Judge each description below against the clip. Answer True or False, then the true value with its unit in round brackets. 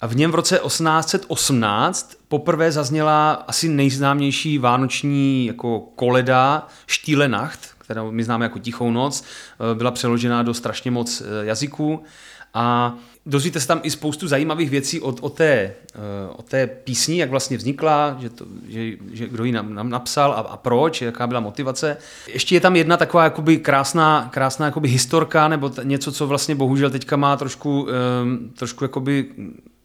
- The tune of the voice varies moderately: True (4.0 semitones)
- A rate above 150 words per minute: True (160 wpm)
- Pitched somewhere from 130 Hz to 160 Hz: True (135 Hz)